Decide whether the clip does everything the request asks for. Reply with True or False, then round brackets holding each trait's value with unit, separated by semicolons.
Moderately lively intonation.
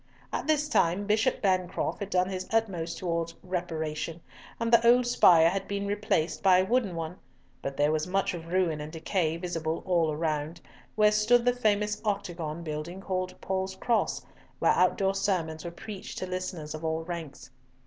True (3.7 semitones)